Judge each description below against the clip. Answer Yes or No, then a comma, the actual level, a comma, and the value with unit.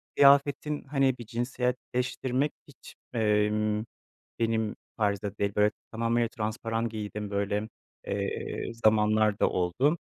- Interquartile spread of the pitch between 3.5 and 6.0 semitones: No, average, 3.1 semitones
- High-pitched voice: No, low, 110 Hz